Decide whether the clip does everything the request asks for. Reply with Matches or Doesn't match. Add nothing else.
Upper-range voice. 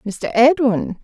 Matches